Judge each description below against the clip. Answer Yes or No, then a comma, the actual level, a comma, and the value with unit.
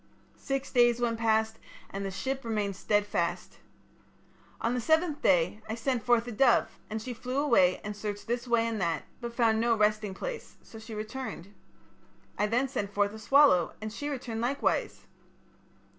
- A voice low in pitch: No, high, 225 Hz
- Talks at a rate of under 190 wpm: Yes, average, 175 wpm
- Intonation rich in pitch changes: No, average, 2.9 semitones